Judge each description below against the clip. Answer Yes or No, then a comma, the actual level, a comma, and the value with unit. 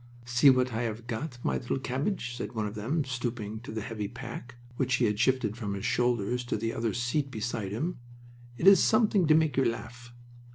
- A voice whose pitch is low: Yes, low, 120 Hz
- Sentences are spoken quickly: Yes, fast, 210 wpm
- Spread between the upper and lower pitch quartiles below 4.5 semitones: Yes, average, 2.9 semitones